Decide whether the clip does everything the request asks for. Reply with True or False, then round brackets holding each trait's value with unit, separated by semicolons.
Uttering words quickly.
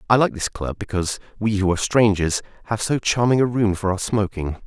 True (220 wpm)